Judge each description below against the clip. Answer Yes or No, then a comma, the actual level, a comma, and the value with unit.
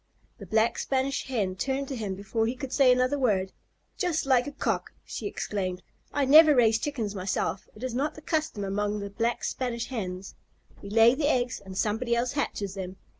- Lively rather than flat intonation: No, average, 4.9 semitones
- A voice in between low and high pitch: No, high, 235 Hz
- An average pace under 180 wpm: No, average, 195 wpm